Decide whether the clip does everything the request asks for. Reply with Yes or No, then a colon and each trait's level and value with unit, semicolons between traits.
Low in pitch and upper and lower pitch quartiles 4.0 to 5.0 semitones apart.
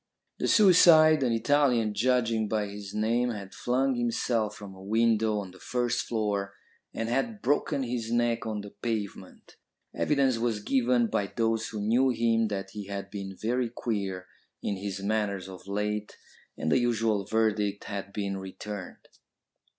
No: low, 110 Hz; average, 3.1 semitones